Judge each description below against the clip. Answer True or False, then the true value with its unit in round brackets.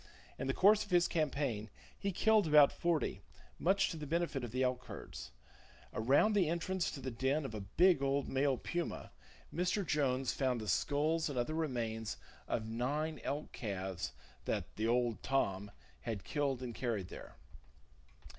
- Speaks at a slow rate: False (165 wpm)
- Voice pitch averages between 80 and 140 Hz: True (135 Hz)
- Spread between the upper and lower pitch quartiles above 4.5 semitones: True (5.4 semitones)